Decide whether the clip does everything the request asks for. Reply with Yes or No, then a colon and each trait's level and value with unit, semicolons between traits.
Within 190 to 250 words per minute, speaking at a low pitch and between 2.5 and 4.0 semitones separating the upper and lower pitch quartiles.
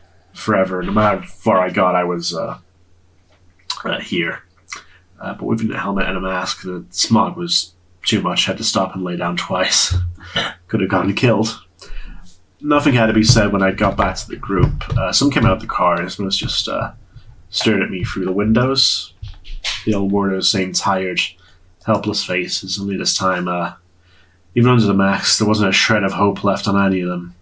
Yes: average, 200 wpm; very low, 95 Hz; average, 2.9 semitones